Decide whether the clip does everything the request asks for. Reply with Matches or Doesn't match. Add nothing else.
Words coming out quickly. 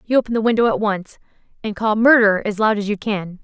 Matches